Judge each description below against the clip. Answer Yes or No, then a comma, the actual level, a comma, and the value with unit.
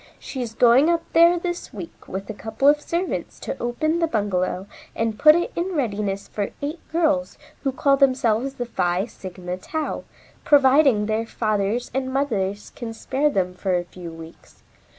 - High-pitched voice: Yes, high, 240 Hz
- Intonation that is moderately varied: No, wide, 6.5 semitones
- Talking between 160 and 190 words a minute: Yes, average, 170 wpm